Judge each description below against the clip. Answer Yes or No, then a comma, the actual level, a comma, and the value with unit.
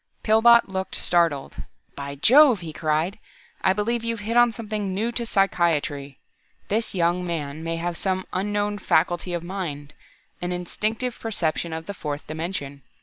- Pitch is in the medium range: Yes, medium, 180 Hz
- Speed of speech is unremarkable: Yes, average, 150 wpm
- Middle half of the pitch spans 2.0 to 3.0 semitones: No, average, 4.8 semitones